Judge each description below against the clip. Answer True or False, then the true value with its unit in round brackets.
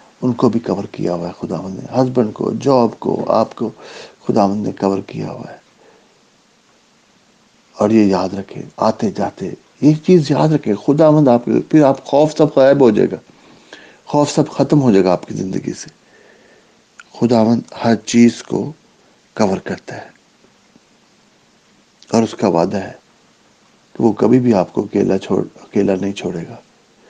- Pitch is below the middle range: True (120 Hz)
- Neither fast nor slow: True (180 wpm)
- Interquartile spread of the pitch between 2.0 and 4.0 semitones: False (5.3 semitones)